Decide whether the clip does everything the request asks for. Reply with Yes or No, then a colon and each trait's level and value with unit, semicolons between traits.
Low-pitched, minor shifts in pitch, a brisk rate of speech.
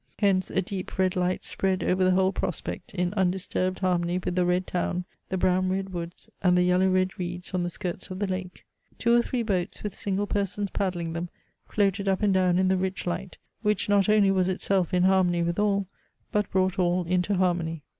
No: medium, 185 Hz; narrow, 1.4 semitones; fast, 210 wpm